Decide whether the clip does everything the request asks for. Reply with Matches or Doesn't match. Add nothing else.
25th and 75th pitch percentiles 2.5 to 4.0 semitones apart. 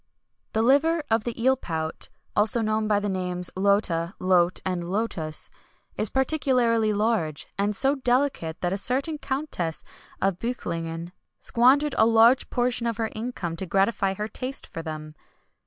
Doesn't match